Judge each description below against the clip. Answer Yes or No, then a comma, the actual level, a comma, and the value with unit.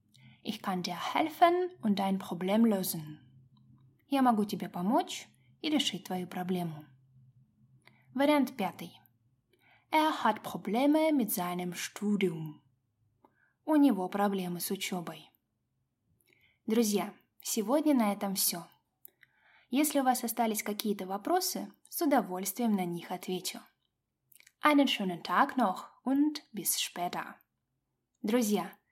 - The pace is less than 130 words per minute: Yes, slow, 110 wpm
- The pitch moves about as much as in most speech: No, wide, 6.3 semitones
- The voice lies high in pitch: Yes, high, 195 Hz